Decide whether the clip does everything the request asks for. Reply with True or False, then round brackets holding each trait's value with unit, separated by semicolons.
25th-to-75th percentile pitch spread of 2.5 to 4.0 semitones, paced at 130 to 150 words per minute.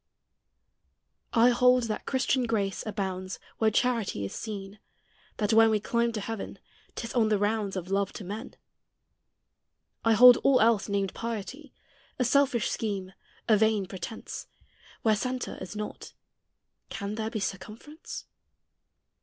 True (2.9 semitones; 140 wpm)